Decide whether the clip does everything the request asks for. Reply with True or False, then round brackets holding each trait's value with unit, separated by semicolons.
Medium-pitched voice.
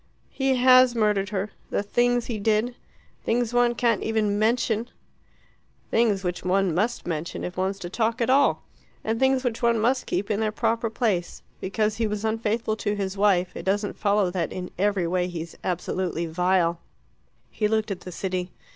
False (210 Hz)